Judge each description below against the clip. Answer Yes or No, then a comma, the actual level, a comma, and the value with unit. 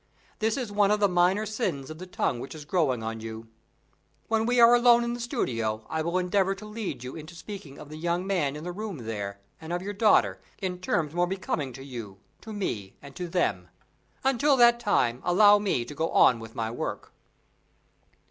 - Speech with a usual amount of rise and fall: No, wide, 8.3 semitones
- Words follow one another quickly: Yes, fast, 210 wpm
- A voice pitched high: No, medium, 175 Hz